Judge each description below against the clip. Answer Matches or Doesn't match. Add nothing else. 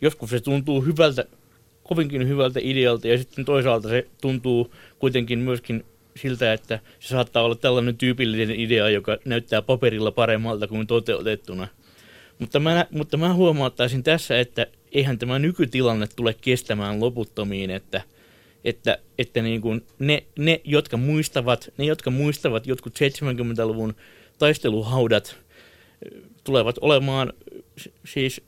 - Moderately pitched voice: Doesn't match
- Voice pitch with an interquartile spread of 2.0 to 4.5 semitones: Matches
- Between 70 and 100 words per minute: Doesn't match